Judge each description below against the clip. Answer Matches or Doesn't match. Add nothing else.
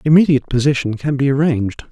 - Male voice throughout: Matches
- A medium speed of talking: Matches